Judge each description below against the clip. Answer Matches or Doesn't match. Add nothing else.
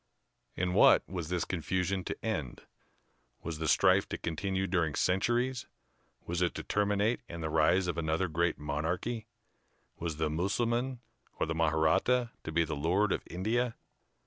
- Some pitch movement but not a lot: Matches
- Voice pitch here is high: Doesn't match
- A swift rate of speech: Doesn't match